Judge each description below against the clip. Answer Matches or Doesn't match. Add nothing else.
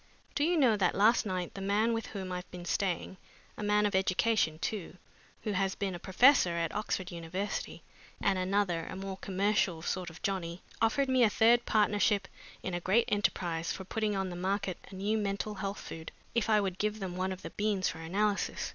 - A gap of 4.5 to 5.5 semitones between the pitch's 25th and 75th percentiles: Doesn't match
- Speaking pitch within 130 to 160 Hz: Doesn't match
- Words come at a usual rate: Doesn't match